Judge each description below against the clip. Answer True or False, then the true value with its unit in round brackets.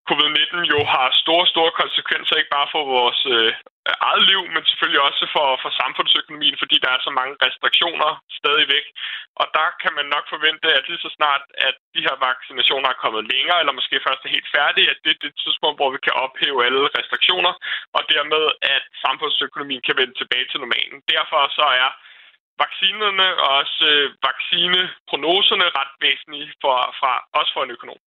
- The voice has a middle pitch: True (155 Hz)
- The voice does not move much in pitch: False (3.6 semitones)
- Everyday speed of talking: True (180 wpm)